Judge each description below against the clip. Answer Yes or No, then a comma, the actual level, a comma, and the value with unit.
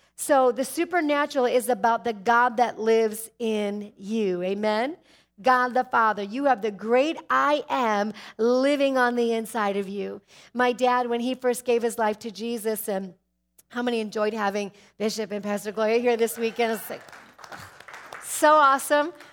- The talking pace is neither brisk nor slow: Yes, average, 165 wpm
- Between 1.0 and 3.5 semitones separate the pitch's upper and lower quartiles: Yes, average, 2.8 semitones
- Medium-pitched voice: No, high, 230 Hz